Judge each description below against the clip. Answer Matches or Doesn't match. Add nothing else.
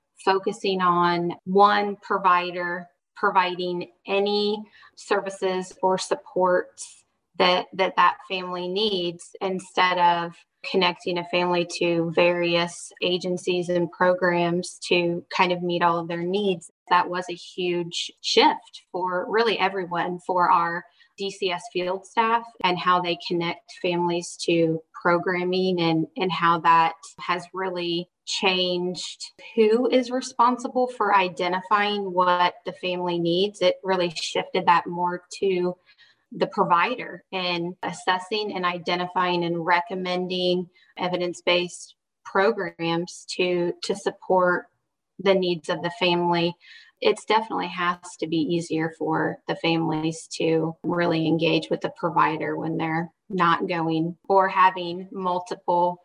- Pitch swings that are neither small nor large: Doesn't match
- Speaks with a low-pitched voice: Doesn't match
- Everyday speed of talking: Doesn't match